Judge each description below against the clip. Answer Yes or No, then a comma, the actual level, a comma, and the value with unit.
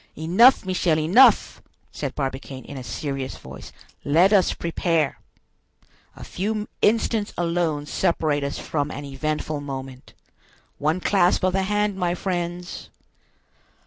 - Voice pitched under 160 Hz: No, medium, 165 Hz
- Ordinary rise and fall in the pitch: Yes, average, 4.6 semitones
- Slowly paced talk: Yes, slow, 125 wpm